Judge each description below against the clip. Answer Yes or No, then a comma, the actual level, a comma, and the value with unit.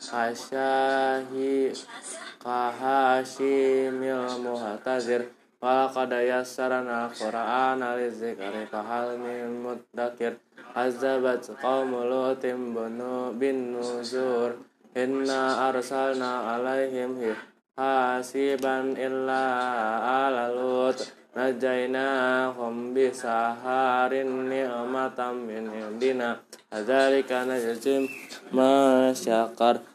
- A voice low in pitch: Yes, low, 125 Hz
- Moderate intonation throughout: No, narrow, 1.5 semitones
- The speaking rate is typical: No, slow, 55 wpm